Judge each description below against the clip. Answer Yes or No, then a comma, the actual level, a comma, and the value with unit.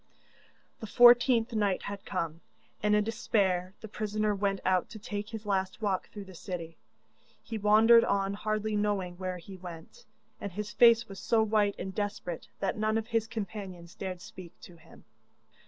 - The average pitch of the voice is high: Yes, high, 205 Hz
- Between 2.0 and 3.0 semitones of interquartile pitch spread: Yes, narrow, 2.6 semitones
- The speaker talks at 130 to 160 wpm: No, average, 170 wpm